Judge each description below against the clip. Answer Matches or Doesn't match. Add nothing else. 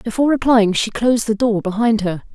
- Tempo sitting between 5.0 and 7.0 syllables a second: Matches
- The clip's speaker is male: Doesn't match